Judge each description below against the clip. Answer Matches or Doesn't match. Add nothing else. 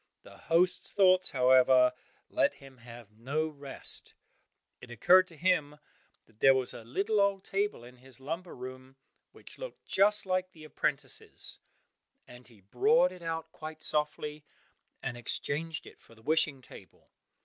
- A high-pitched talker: Doesn't match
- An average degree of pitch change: Doesn't match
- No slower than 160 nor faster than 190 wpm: Doesn't match